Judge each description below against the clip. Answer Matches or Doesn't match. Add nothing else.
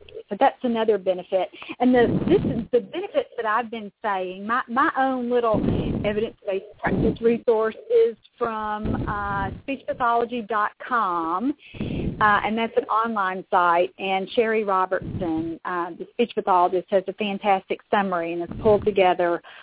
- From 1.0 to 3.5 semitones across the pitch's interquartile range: Doesn't match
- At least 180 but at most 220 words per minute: Doesn't match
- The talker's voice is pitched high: Matches